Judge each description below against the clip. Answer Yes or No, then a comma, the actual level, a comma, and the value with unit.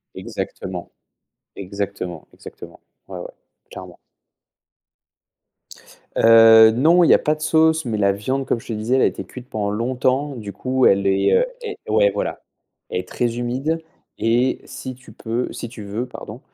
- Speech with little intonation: No, average, 4.4 semitones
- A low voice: Yes, low, 115 Hz